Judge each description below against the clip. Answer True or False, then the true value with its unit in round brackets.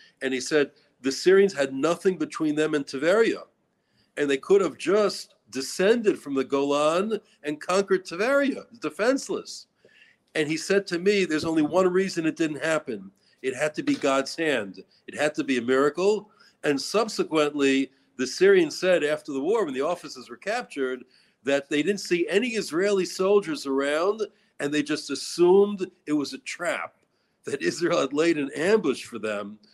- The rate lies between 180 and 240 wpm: False (170 wpm)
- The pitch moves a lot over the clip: True (6.0 semitones)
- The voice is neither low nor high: True (160 Hz)